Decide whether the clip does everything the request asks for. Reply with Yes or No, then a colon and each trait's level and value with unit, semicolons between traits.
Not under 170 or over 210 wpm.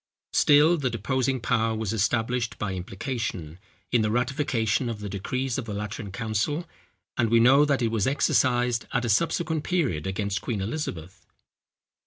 No: average, 160 wpm